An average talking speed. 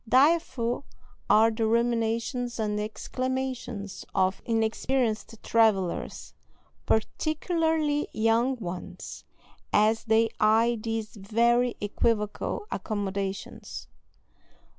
No: slow, 75 wpm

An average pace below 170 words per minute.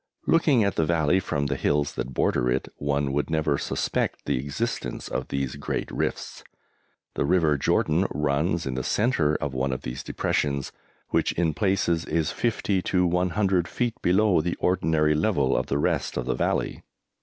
No: average, 175 wpm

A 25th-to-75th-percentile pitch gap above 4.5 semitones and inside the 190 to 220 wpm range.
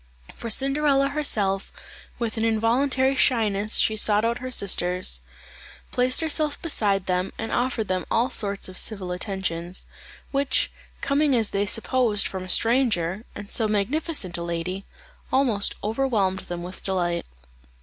No: average, 5.3 semitones; average, 140 wpm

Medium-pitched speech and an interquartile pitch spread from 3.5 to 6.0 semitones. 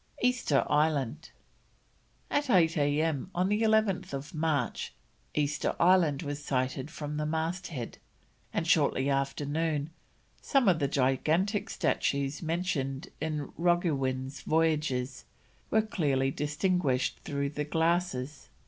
Yes: medium, 150 Hz; average, 3.9 semitones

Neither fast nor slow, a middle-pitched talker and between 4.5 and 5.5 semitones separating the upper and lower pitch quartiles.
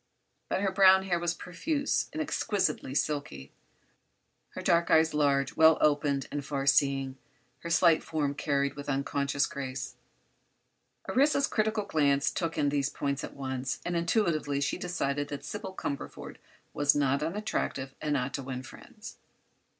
No: average, 150 wpm; medium, 145 Hz; average, 3.6 semitones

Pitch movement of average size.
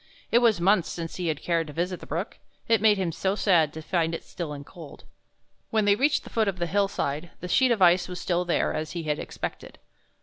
Yes: average, 3.6 semitones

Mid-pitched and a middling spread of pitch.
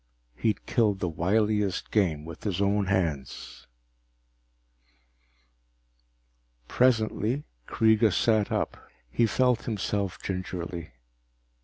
No: low, 100 Hz; average, 3.5 semitones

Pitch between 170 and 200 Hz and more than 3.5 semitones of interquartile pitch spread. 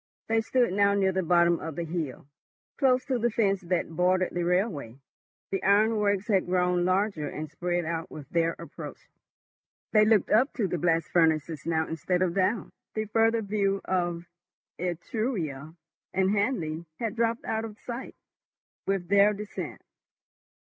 Yes: medium, 185 Hz; average, 3.9 semitones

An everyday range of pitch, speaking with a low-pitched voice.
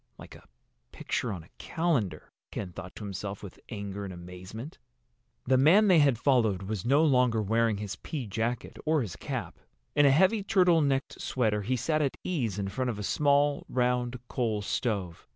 No: wide, 5.8 semitones; low, 120 Hz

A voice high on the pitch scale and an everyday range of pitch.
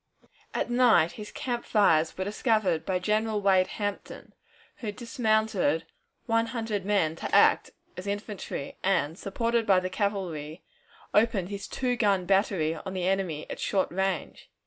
Yes: high, 200 Hz; average, 3.0 semitones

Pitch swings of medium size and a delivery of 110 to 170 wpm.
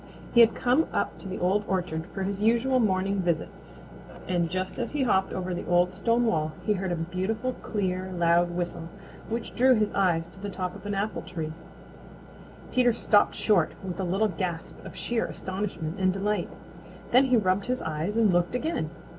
No: average, 3.8 semitones; average, 190 wpm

